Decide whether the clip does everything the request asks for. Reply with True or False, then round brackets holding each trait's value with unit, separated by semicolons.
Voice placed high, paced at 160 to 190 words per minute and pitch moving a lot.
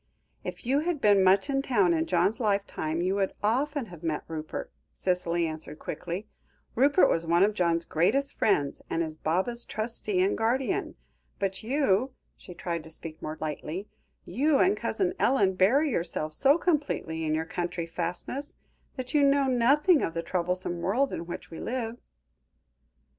True (195 Hz; 165 wpm; 7.6 semitones)